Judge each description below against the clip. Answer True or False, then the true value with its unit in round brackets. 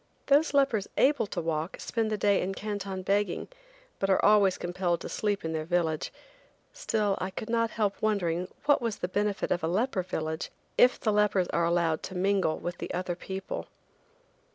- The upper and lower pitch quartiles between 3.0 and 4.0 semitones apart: True (3.3 semitones)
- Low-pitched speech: False (195 Hz)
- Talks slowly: False (185 wpm)